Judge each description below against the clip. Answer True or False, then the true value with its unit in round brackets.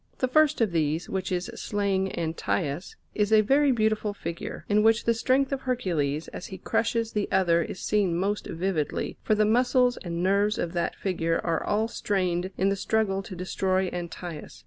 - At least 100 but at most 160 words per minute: False (185 wpm)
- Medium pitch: False (195 Hz)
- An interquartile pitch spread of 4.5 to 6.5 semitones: False (4.1 semitones)